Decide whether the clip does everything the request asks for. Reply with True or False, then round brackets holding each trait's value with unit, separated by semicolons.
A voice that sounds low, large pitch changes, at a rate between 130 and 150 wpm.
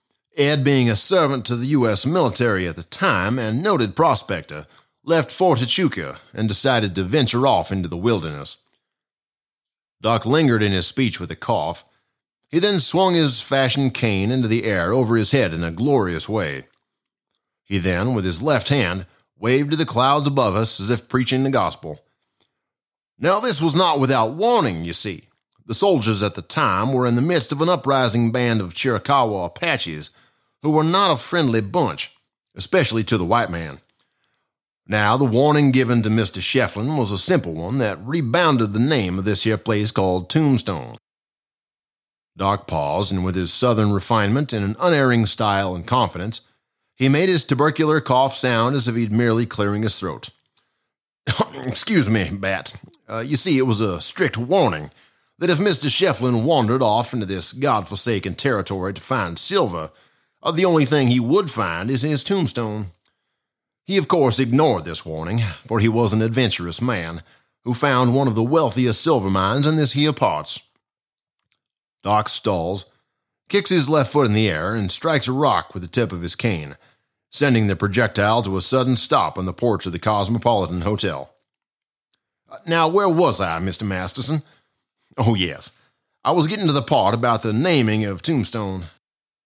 False (120 Hz; 5.7 semitones; 175 wpm)